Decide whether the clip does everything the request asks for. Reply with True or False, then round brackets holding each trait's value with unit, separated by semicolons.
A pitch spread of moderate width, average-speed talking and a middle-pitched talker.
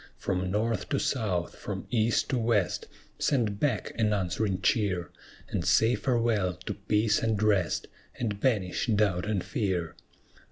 False (3.4 semitones; 145 wpm; 105 Hz)